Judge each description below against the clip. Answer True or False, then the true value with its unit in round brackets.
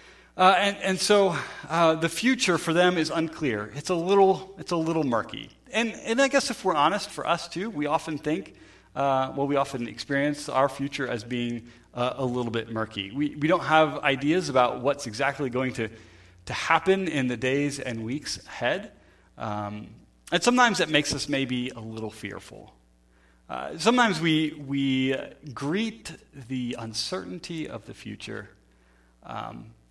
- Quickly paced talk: False (175 wpm)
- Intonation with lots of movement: True (5.7 semitones)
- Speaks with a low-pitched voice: False (145 Hz)